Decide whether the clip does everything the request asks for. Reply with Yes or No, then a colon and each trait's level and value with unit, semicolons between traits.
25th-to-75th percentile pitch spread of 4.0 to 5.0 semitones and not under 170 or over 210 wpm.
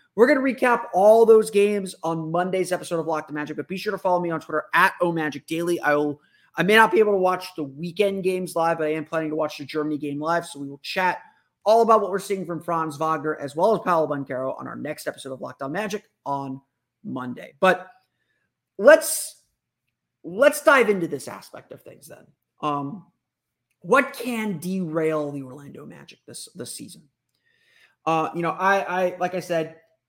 Yes: average, 4.4 semitones; fast, 205 wpm